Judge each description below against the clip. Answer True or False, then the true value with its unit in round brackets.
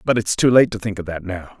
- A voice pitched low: True (100 Hz)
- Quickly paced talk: True (340 wpm)